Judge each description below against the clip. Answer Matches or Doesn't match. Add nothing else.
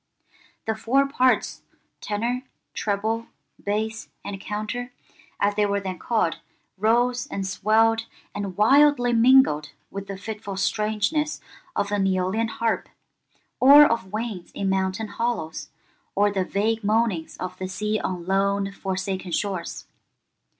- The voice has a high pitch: Matches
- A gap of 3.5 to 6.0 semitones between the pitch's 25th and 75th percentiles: Doesn't match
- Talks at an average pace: Doesn't match